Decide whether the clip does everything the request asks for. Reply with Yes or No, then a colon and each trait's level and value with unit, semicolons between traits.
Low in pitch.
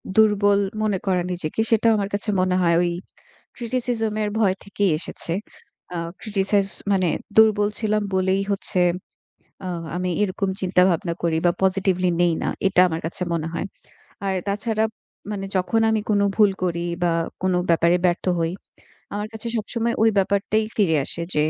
No: high, 195 Hz